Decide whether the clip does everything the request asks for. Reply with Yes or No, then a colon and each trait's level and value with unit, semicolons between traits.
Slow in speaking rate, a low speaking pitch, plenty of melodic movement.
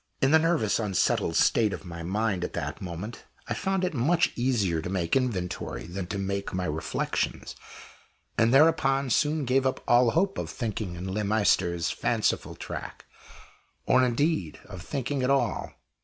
No: average, 170 wpm; low, 110 Hz; wide, 6.7 semitones